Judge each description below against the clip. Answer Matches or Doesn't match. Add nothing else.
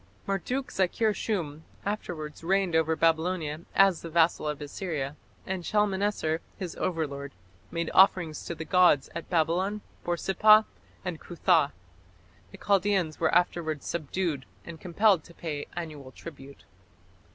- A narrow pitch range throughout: Doesn't match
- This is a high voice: Doesn't match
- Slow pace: Matches